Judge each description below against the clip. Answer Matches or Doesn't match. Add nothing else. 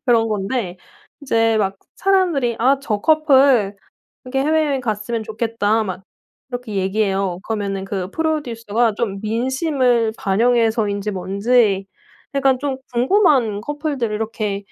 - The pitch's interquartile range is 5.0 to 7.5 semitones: Doesn't match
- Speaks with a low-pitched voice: Doesn't match